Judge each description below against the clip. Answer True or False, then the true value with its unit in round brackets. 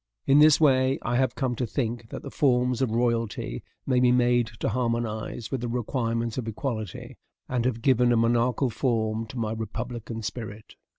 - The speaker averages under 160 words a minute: False (180 wpm)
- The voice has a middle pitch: False (120 Hz)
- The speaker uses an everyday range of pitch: False (1.9 semitones)